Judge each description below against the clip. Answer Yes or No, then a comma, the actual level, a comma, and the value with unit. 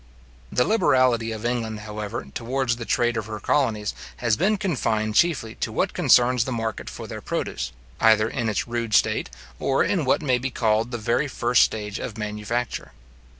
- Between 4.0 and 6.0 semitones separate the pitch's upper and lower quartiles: No, average, 2.8 semitones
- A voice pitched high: No, low, 115 Hz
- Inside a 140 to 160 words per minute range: No, average, 180 wpm